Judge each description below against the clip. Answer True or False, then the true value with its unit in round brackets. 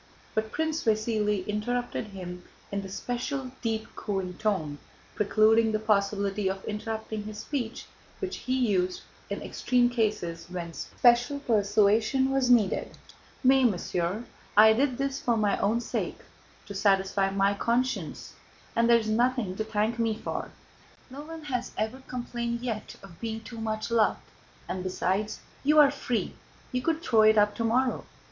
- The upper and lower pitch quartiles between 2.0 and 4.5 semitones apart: True (3.3 semitones)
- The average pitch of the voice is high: True (220 Hz)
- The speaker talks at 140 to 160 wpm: True (155 wpm)